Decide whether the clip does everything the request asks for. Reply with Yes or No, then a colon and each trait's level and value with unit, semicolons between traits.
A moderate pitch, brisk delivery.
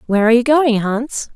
No: high, 240 Hz; fast, 220 wpm